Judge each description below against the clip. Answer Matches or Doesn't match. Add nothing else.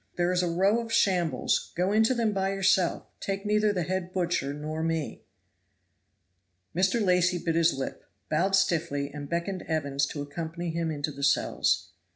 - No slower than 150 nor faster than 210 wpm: Matches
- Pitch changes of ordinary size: Matches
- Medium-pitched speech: Matches